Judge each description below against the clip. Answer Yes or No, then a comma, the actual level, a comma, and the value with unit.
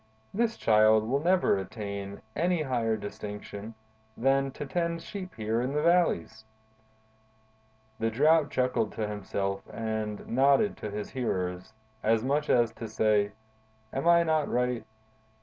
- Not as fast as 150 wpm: Yes, slow, 135 wpm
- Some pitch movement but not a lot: No, wide, 5.8 semitones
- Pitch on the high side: No, low, 115 Hz